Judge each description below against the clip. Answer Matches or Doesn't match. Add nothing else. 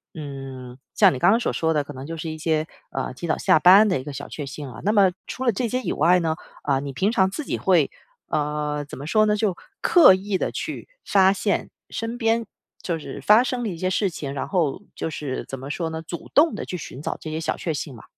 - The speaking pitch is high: Doesn't match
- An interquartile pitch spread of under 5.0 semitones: Doesn't match